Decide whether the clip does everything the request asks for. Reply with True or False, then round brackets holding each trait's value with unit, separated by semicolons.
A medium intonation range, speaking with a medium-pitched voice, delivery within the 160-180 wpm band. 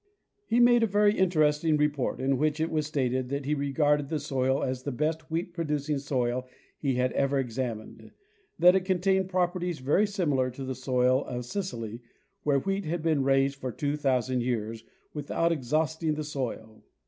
True (4.0 semitones; 145 Hz; 175 wpm)